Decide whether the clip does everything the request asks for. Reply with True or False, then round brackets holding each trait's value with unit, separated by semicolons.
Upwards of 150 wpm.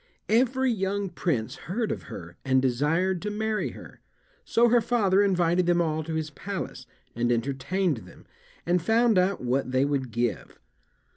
True (160 wpm)